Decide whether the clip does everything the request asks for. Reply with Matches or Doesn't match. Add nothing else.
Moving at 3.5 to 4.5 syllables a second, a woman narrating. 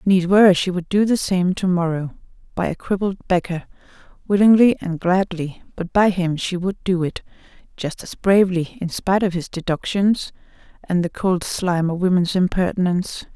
Doesn't match